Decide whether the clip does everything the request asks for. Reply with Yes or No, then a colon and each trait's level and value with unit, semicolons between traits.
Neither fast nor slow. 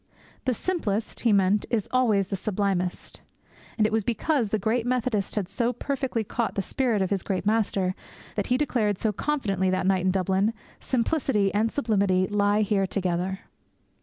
Yes: average, 170 wpm